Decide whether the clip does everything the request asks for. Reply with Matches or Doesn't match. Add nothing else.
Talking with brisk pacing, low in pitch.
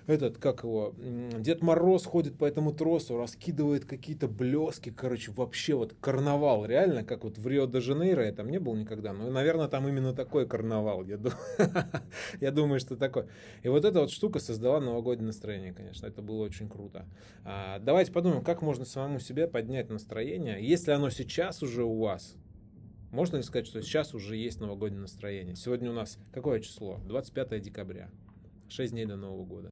Matches